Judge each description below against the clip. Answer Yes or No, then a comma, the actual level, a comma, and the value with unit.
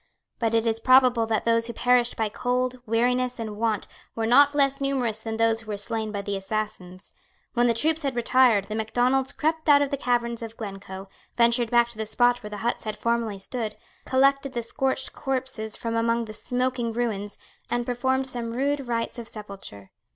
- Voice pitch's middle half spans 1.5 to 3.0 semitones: Yes, narrow, 2.6 semitones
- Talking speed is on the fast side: No, average, 195 wpm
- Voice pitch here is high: Yes, high, 235 Hz